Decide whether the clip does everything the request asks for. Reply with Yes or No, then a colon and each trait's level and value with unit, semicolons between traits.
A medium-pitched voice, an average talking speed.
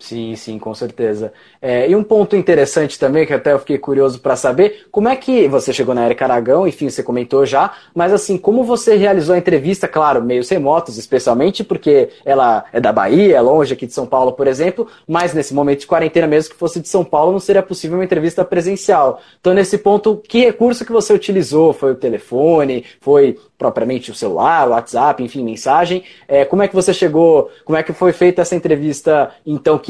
No: medium, 175 Hz; fast, 205 wpm